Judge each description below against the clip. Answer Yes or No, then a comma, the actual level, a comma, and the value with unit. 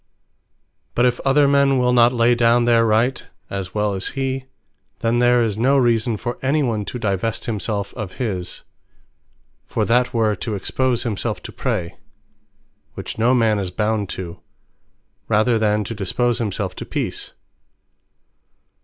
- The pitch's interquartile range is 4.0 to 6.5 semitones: No, average, 2.8 semitones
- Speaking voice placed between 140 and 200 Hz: No, low, 115 Hz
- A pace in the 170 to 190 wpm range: No, average, 155 wpm